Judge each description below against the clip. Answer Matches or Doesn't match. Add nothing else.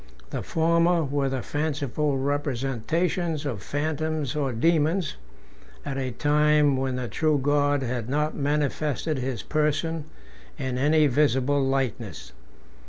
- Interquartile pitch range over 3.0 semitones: Doesn't match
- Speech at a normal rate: Doesn't match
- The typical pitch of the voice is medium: Matches